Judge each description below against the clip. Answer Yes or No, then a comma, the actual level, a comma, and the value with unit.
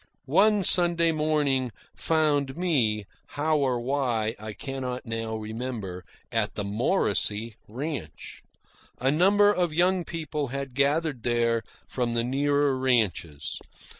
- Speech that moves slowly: Yes, slow, 120 wpm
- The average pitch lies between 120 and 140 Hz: Yes, low, 135 Hz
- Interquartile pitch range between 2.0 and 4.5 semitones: No, average, 5.1 semitones